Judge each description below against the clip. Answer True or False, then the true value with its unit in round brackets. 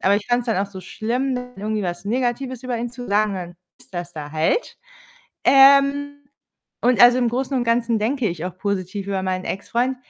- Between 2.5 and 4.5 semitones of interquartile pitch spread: False (5.0 semitones)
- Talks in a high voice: True (225 Hz)